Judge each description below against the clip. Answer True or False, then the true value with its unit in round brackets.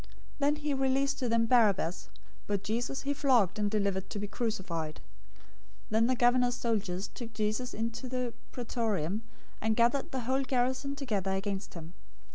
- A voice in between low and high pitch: False (230 Hz)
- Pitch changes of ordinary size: True (4.0 semitones)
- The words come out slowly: False (165 wpm)